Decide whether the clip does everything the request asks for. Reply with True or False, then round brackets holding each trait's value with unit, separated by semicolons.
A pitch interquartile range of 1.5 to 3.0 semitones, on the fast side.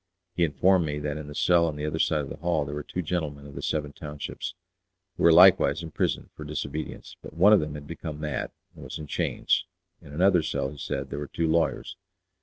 True (2.5 semitones; 230 wpm)